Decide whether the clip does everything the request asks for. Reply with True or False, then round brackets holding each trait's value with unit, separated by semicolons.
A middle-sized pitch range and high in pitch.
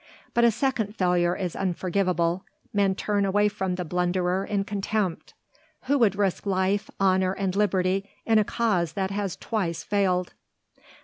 False (2.1 semitones; 195 Hz)